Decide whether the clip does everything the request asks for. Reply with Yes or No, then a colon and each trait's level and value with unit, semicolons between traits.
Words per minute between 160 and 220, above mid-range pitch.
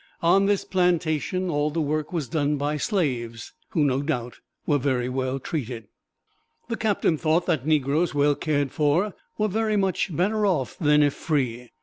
No: average, 165 wpm; medium, 150 Hz